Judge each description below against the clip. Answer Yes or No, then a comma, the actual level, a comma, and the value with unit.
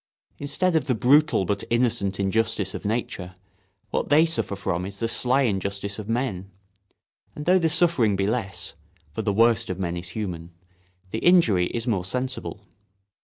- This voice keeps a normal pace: Yes, average, 160 wpm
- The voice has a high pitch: No, low, 105 Hz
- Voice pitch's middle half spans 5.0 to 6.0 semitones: Yes, wide, 5.4 semitones